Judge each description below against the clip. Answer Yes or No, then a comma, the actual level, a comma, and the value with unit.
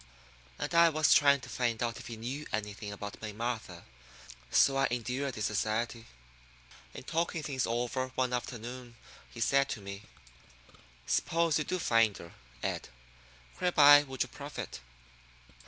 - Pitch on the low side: Yes, low, 125 Hz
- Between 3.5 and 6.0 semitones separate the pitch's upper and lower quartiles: Yes, average, 3.9 semitones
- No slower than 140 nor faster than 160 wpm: Yes, average, 150 wpm